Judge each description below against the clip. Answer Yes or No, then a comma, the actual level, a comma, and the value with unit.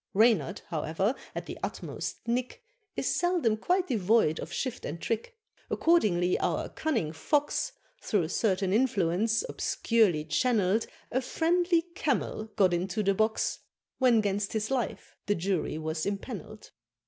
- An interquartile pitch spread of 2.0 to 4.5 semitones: No, wide, 5.5 semitones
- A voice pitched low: No, high, 215 Hz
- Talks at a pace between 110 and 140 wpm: Yes, slow, 135 wpm